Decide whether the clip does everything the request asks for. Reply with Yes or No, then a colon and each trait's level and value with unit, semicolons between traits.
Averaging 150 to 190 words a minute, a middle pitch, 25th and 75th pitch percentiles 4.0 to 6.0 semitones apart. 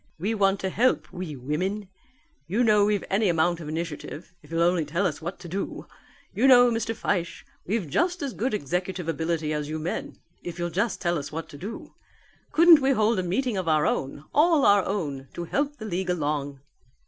No: fast, 205 wpm; medium, 180 Hz; average, 5.2 semitones